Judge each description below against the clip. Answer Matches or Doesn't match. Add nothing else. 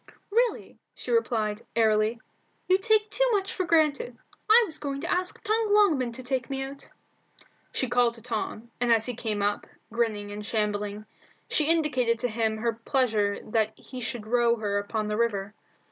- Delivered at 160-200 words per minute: Matches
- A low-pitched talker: Doesn't match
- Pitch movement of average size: Doesn't match